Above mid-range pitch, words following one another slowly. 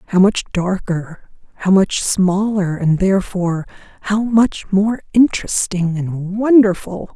Yes: high, 195 Hz; slow, 115 wpm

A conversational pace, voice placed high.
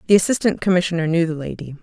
No: average, 195 wpm; medium, 175 Hz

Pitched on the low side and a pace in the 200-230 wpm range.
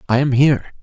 Yes: low, 130 Hz; fast, 220 wpm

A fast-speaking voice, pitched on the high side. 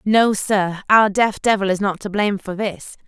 Yes: fast, 215 wpm; high, 200 Hz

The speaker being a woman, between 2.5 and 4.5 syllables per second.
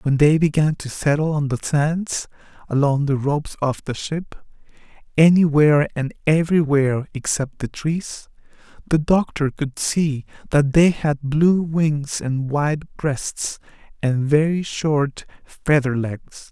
No: male; 4.0 syllables/s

